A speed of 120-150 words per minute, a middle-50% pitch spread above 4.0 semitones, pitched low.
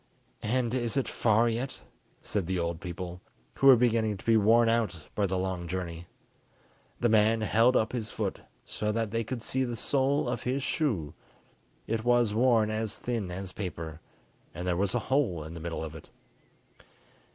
No: average, 185 wpm; average, 4.6 semitones; low, 110 Hz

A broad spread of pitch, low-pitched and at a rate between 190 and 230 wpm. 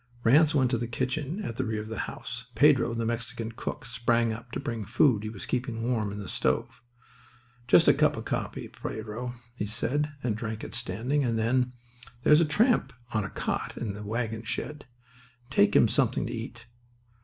No: average, 2.9 semitones; low, 115 Hz; average, 200 wpm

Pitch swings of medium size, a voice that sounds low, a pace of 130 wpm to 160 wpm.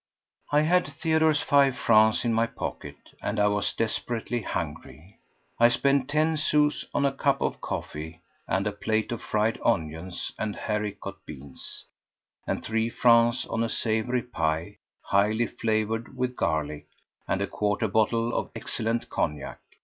Yes: average, 4.0 semitones; low, 110 Hz; average, 150 wpm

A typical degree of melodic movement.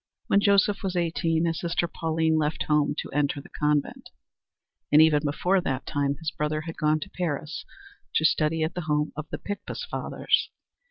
No: narrow, 2.1 semitones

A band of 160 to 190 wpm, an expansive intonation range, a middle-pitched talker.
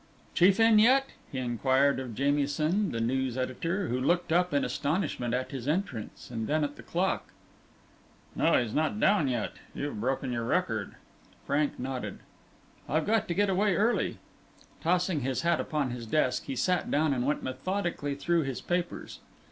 Yes: average, 170 wpm; wide, 5.7 semitones; medium, 145 Hz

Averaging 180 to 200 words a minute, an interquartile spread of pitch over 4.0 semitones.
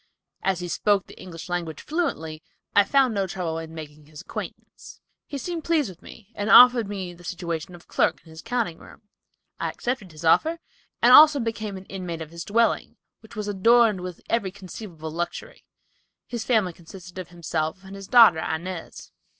Yes: average, 185 wpm; average, 5.2 semitones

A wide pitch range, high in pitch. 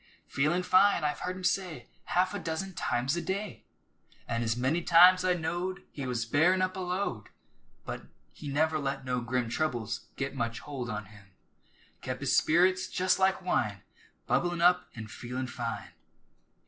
No: wide, 6.7 semitones; medium, 155 Hz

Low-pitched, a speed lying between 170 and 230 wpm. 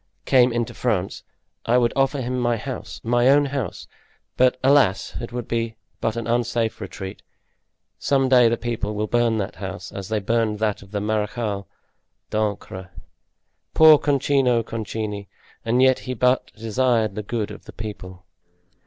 No: low, 115 Hz; average, 155 wpm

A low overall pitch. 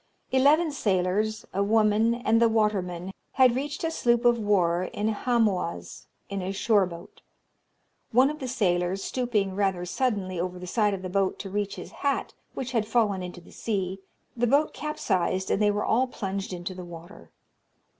No: high, 205 Hz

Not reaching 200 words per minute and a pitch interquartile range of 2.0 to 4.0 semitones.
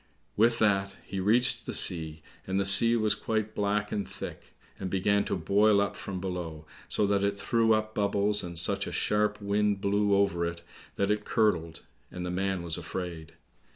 Yes: average, 190 wpm; average, 2.7 semitones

